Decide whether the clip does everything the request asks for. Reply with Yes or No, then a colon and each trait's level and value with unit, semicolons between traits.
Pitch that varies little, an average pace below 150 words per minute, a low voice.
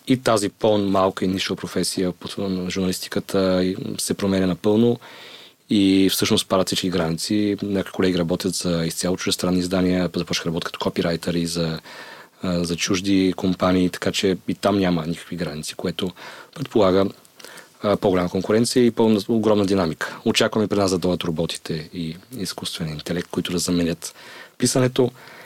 Yes: narrow, 2.3 semitones; average, 140 wpm; very low, 95 Hz